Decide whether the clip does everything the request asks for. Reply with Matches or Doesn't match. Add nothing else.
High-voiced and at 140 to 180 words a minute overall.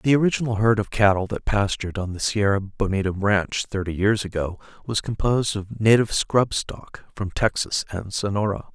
Doesn't match